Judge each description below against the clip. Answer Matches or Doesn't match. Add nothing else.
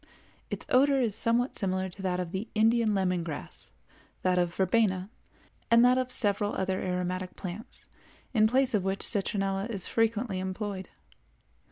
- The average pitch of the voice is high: Matches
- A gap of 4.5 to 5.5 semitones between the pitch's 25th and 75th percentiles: Doesn't match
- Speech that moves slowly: Doesn't match